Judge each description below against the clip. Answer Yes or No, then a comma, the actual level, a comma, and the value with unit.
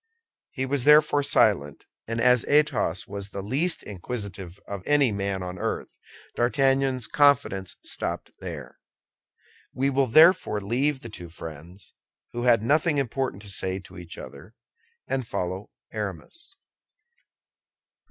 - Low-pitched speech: Yes, low, 115 Hz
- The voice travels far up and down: Yes, wide, 6.1 semitones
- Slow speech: Yes, slow, 130 wpm